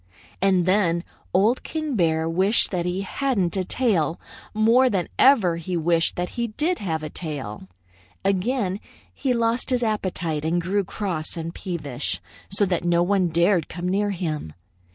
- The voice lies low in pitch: No, medium, 185 Hz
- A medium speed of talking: Yes, average, 160 wpm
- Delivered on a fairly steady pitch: No, average, 4.0 semitones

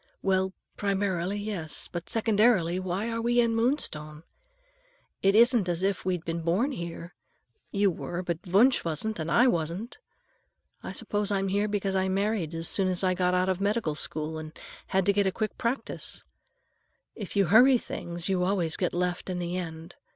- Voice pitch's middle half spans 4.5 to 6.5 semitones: No, average, 3.4 semitones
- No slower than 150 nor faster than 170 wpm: No, average, 180 wpm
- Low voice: No, high, 190 Hz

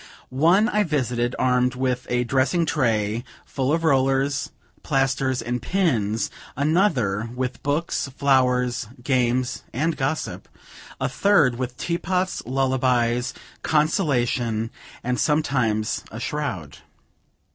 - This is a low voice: Yes, low, 130 Hz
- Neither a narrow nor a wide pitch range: Yes, average, 3.5 semitones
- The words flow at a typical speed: No, slow, 105 wpm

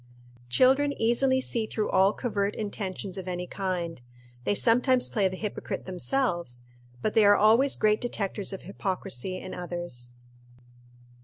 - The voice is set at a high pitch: Yes, high, 200 Hz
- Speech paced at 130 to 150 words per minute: Yes, average, 140 wpm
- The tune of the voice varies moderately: Yes, average, 3.9 semitones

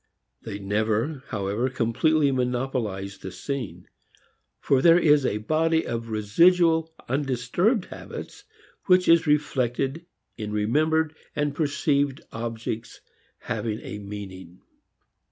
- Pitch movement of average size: No, wide, 6.5 semitones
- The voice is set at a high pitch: No, low, 130 Hz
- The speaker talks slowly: Yes, slow, 105 wpm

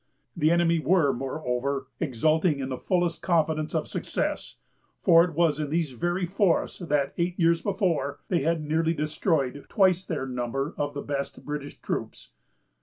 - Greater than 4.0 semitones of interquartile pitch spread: No, average, 3.4 semitones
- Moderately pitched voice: Yes, medium, 155 Hz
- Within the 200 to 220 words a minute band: No, average, 160 wpm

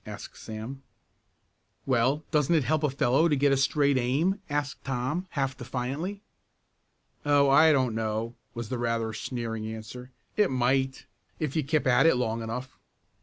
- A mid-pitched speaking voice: No, low, 130 Hz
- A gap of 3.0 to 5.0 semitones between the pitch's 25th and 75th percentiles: Yes, average, 3.4 semitones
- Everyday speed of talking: Yes, average, 160 wpm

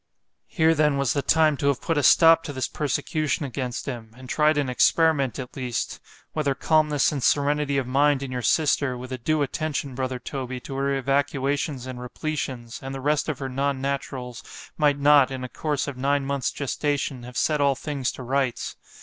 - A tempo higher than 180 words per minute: Yes, average, 190 wpm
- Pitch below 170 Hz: Yes, medium, 140 Hz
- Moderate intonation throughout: No, narrow, 2.3 semitones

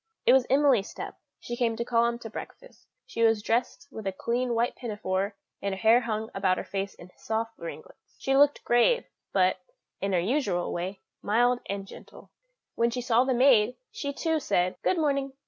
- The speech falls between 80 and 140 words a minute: No, average, 195 wpm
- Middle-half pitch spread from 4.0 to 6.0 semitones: Yes, average, 4.3 semitones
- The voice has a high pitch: Yes, high, 230 Hz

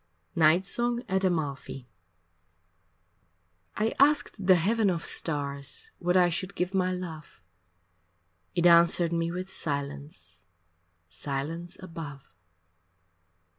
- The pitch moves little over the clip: No, average, 4.2 semitones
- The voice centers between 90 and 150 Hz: No, medium, 170 Hz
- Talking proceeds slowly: Yes, slow, 105 wpm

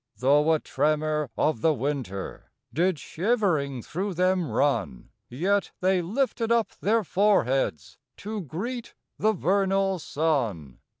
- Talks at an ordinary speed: No, slow, 125 wpm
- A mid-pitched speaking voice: Yes, medium, 165 Hz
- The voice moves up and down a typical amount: No, wide, 6.0 semitones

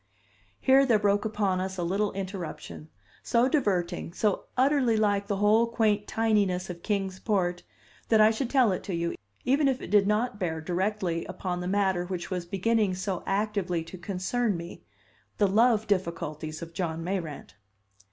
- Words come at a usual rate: Yes, average, 170 wpm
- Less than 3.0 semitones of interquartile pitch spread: No, average, 3.4 semitones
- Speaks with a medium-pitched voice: No, high, 195 Hz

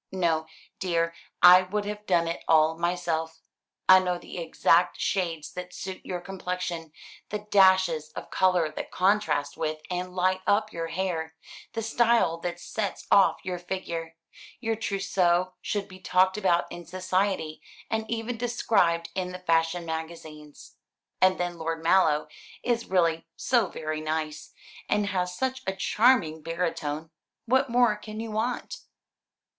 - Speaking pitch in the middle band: Yes, medium, 180 Hz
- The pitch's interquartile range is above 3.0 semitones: Yes, average, 3.4 semitones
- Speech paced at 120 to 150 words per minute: Yes, average, 145 wpm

